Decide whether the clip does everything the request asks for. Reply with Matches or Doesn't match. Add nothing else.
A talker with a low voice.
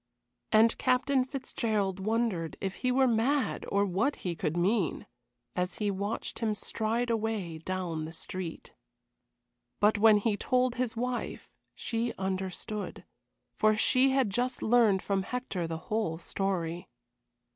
Doesn't match